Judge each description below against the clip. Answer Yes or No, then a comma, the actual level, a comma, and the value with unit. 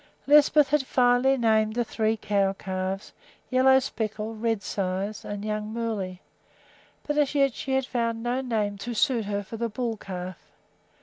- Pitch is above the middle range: Yes, high, 225 Hz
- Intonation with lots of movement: No, average, 3.9 semitones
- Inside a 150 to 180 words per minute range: Yes, average, 160 wpm